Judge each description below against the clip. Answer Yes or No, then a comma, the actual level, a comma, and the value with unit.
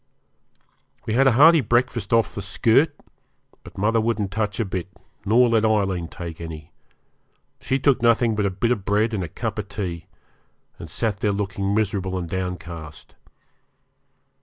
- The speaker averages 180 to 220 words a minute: No, average, 160 wpm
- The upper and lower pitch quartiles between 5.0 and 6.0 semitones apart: No, average, 3.9 semitones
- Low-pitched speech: Yes, low, 105 Hz